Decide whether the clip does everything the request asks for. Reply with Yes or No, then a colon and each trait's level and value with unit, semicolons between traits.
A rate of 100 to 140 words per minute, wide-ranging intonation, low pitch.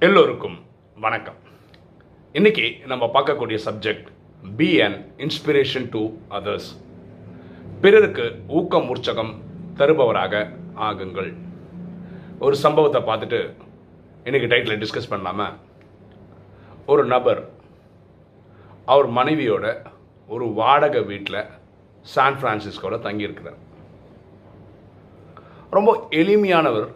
No: average, 80 wpm; wide, 8.5 semitones; low, 115 Hz